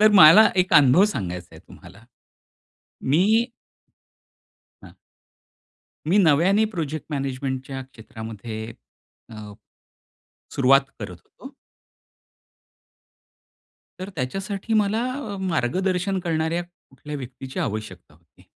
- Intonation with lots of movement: Yes, wide, 7.1 semitones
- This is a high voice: No, medium, 150 Hz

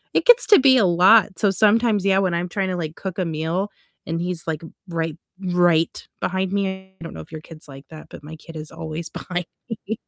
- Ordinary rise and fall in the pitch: Yes, average, 3.2 semitones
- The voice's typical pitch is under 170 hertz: No, medium, 180 Hz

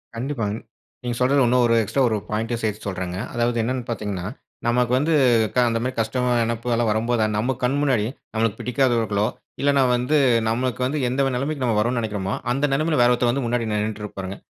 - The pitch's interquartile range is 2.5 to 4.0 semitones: Yes, average, 2.8 semitones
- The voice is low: Yes, low, 120 Hz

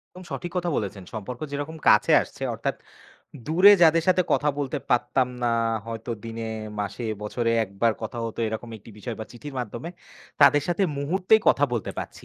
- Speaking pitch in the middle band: No, low, 125 Hz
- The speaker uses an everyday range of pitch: No, wide, 6.1 semitones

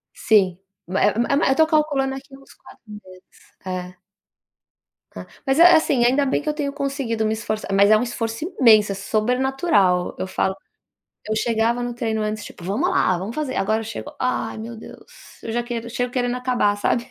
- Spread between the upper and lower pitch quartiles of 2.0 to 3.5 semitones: No, average, 3.9 semitones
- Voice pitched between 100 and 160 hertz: No, high, 230 Hz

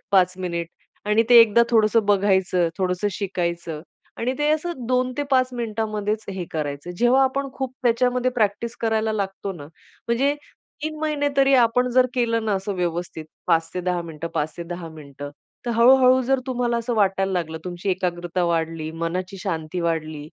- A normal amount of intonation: No, wide, 5.9 semitones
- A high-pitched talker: Yes, high, 200 Hz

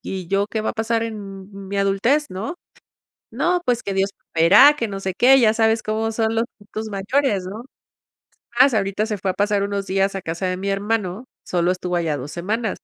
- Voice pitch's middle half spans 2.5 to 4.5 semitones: Yes, average, 2.8 semitones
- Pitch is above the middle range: Yes, high, 200 Hz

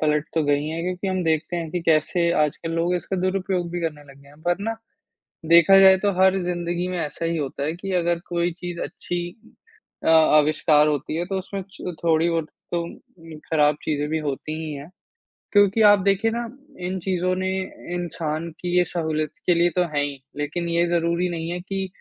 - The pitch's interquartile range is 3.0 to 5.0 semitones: No, narrow, 2.6 semitones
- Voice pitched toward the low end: No, medium, 170 Hz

